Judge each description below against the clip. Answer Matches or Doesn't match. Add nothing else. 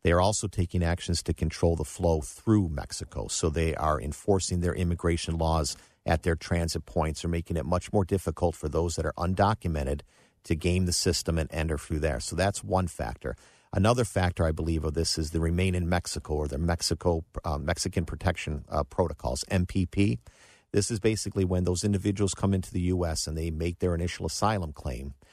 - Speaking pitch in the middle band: Doesn't match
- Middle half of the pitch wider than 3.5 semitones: Doesn't match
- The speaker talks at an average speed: Matches